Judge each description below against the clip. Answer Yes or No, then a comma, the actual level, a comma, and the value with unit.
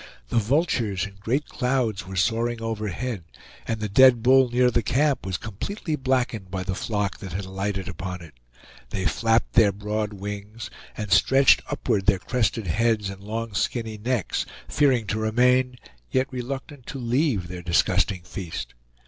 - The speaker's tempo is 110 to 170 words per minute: Yes, average, 160 wpm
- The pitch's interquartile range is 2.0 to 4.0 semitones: No, average, 4.5 semitones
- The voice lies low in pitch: Yes, low, 110 Hz